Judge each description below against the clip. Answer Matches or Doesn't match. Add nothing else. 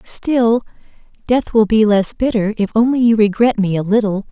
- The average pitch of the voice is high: Matches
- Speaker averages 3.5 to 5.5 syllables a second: Matches